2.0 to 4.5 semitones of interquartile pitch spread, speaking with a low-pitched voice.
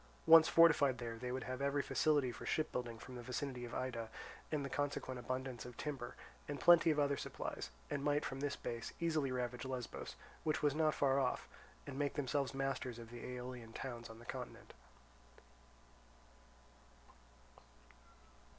Yes: average, 2.8 semitones; low, 130 Hz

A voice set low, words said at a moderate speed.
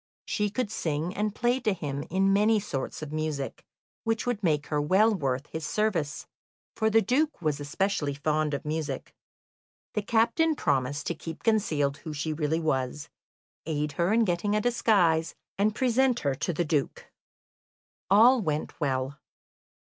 No: medium, 165 Hz; average, 160 wpm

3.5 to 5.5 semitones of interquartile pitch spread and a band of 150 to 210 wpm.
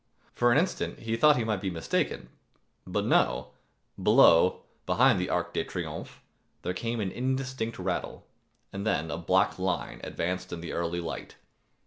Yes: average, 5.0 semitones; average, 160 wpm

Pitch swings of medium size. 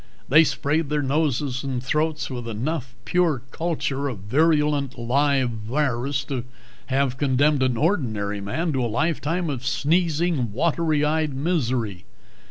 Yes: average, 3.9 semitones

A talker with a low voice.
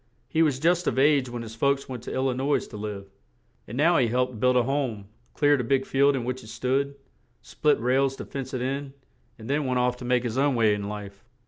Yes: low, 130 Hz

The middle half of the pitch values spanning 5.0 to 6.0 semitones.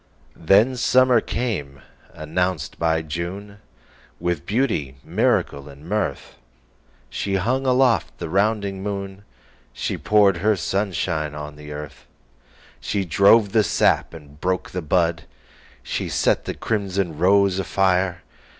Yes: average, 5.3 semitones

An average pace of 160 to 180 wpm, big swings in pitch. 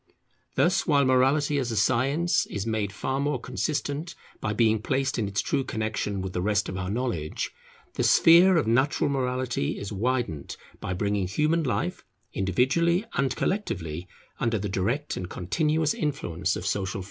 Yes: average, 165 wpm; wide, 6.4 semitones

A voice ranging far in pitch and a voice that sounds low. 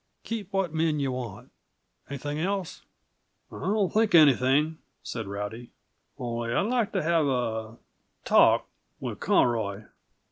No: wide, 7.4 semitones; medium, 145 Hz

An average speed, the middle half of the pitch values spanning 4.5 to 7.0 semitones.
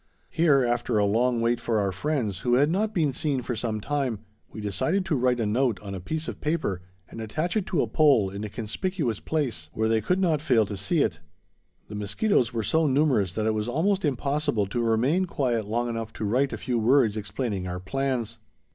No: fast, 220 wpm; wide, 5.5 semitones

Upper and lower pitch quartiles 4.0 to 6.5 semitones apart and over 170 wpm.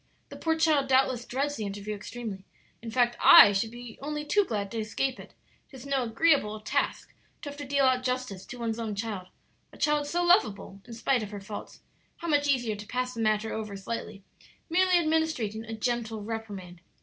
Yes: average, 4.7 semitones; average, 195 wpm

